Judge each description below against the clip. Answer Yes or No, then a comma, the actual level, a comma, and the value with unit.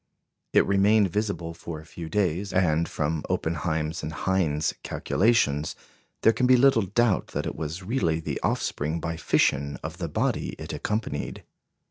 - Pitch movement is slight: No, average, 4.5 semitones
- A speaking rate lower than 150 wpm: No, average, 155 wpm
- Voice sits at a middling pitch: No, very low, 85 Hz